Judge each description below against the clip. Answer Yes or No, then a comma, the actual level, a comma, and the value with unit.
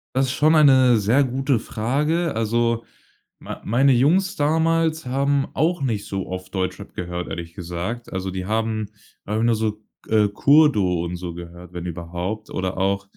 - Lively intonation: Yes, wide, 6.8 semitones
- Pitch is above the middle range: No, low, 110 Hz